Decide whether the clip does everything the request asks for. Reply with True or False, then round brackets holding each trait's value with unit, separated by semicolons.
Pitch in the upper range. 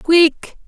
True (330 Hz)